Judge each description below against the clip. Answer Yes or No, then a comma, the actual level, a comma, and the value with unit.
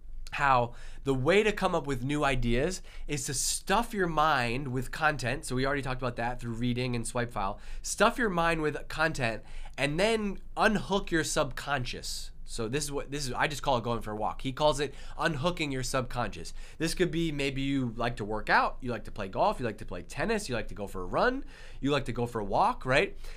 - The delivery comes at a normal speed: No, fast, 235 wpm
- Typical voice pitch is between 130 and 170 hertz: Yes, medium, 140 Hz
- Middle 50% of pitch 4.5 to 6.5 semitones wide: Yes, average, 4.8 semitones